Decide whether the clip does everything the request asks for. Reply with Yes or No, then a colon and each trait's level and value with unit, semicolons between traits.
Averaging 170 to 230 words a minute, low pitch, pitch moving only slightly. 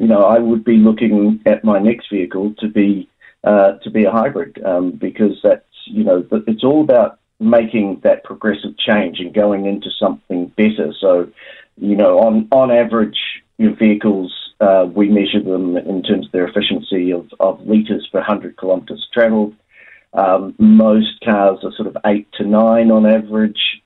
Yes: average, 175 wpm; low, 105 Hz; narrow, 1.9 semitones